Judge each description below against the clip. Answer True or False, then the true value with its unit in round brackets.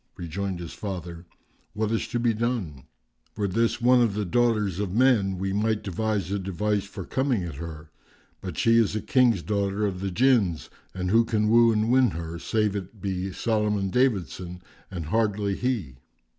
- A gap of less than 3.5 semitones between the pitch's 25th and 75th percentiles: False (3.8 semitones)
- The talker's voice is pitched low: True (100 Hz)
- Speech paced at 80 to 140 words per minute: False (185 wpm)